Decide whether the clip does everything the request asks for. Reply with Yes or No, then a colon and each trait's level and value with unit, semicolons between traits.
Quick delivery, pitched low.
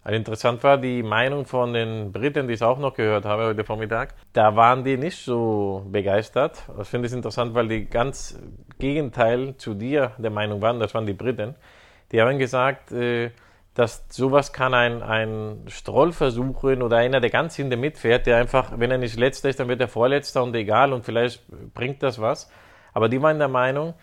Yes: fast, 195 wpm; low, 120 Hz